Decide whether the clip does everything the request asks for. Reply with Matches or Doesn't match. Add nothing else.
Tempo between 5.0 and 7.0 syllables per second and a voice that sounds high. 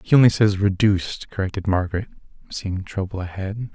Doesn't match